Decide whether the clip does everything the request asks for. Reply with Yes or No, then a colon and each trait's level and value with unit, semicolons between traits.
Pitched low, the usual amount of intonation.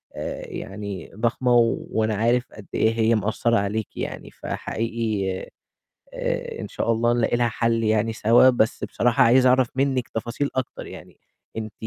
No: low, 115 Hz; narrow, 1.9 semitones